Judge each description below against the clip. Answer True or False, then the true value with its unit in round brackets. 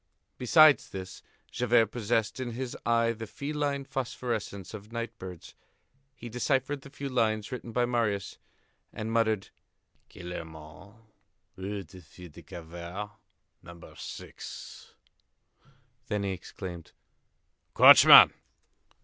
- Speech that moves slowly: True (110 wpm)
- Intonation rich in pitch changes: False (4.6 semitones)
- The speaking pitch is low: True (110 Hz)